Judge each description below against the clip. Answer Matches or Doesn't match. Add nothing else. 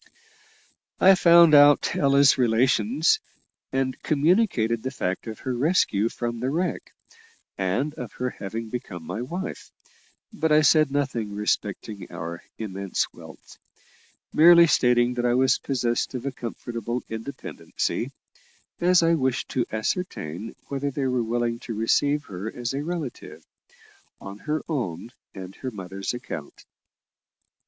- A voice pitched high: Doesn't match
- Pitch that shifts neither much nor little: Matches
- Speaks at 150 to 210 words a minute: Doesn't match